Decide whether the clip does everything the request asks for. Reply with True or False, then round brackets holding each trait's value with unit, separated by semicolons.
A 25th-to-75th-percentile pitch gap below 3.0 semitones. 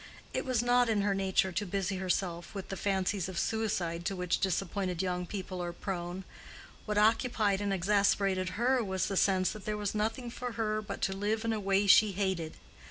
True (2.4 semitones)